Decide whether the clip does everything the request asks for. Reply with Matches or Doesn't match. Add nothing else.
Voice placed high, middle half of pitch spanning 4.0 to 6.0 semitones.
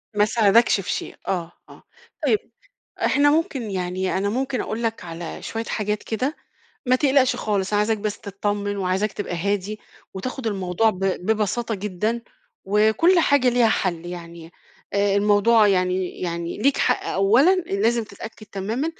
Doesn't match